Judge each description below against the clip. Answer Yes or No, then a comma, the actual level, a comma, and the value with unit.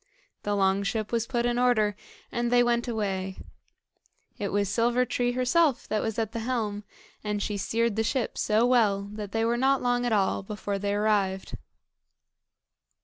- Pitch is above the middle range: Yes, high, 220 Hz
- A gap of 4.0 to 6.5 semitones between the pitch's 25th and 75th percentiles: No, average, 2.9 semitones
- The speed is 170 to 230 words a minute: Yes, average, 175 wpm